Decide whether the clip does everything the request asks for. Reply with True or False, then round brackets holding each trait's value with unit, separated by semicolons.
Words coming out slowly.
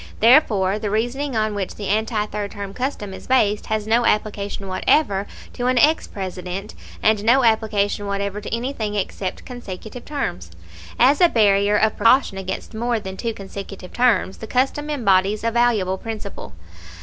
False (160 wpm)